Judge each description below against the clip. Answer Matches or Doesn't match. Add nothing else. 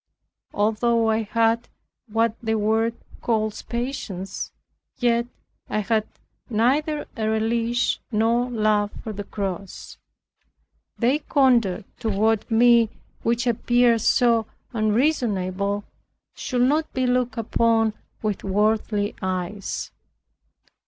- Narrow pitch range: Matches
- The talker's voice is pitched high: Matches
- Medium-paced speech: Doesn't match